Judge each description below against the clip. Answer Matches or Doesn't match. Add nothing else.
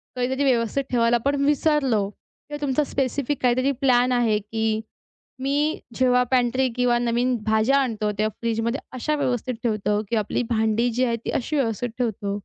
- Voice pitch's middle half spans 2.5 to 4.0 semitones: Matches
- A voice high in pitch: Matches